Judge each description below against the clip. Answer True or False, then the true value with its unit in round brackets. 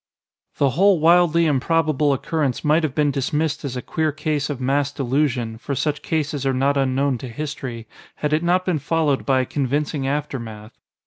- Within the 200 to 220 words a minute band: False (180 wpm)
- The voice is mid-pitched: True (145 Hz)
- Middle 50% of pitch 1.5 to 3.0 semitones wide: True (2.6 semitones)